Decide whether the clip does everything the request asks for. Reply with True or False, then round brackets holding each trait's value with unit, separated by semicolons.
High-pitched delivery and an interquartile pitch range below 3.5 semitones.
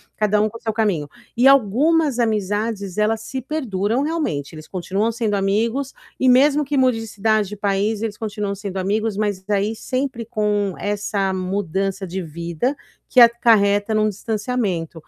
True (210 Hz; 3.0 semitones)